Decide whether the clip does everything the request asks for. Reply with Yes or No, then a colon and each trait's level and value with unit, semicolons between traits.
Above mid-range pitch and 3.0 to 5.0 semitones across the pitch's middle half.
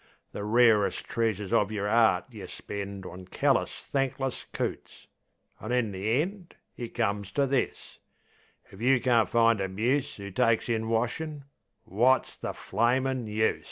No: low, 115 Hz; average, 3.7 semitones